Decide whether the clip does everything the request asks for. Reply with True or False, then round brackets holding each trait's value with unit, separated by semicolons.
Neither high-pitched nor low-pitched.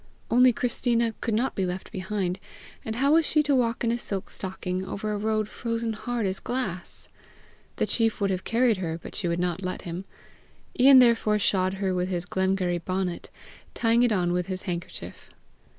False (200 Hz)